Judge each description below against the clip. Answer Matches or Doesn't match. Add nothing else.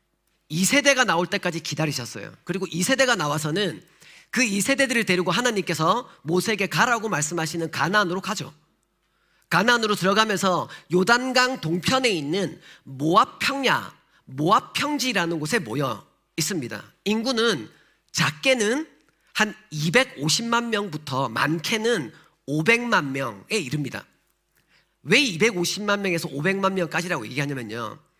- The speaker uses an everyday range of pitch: Doesn't match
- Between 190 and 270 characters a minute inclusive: Doesn't match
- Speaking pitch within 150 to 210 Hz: Matches